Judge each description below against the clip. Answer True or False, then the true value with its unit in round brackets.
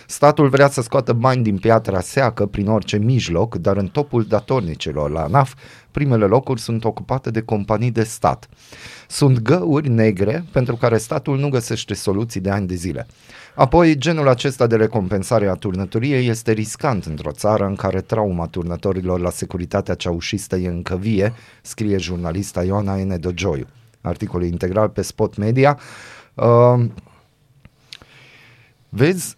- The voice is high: False (110 Hz)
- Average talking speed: True (145 wpm)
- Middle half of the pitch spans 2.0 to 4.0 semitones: False (4.6 semitones)